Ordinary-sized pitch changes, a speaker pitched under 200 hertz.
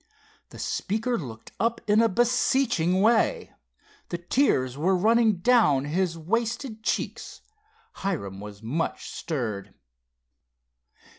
No: wide, 8.2 semitones; medium, 185 Hz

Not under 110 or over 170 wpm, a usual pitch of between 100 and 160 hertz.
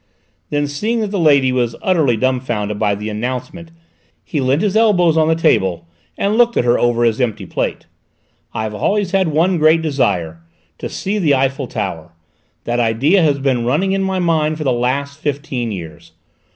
No: average, 185 wpm; medium, 140 Hz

